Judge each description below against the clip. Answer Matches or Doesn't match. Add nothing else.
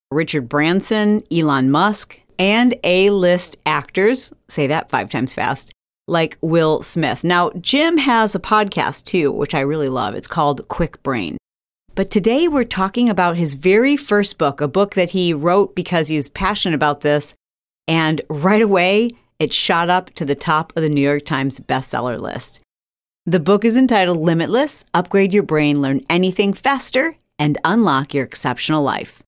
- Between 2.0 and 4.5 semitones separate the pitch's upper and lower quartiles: Doesn't match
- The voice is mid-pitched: Matches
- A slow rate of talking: Doesn't match